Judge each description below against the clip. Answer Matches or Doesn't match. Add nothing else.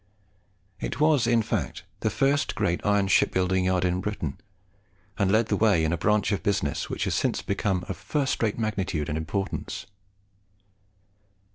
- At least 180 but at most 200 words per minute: Doesn't match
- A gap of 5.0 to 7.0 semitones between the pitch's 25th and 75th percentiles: Doesn't match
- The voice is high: Doesn't match